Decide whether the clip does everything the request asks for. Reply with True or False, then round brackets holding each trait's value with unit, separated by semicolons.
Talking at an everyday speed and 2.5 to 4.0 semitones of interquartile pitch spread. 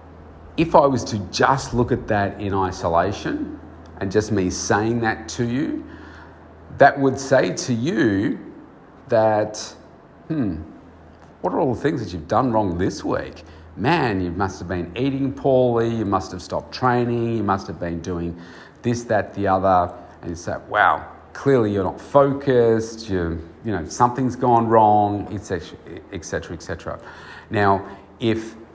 False (155 wpm; 5.0 semitones)